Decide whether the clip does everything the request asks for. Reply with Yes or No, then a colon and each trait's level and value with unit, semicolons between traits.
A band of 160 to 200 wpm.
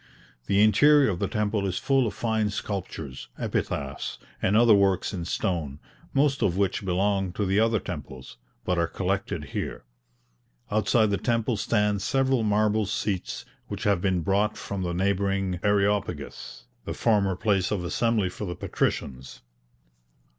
No: average, 150 wpm